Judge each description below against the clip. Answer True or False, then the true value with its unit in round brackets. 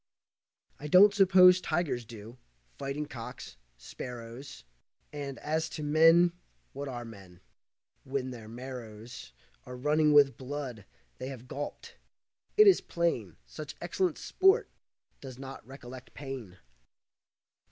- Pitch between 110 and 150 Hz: True (135 Hz)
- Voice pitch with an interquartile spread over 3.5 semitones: True (4.4 semitones)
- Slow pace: True (120 wpm)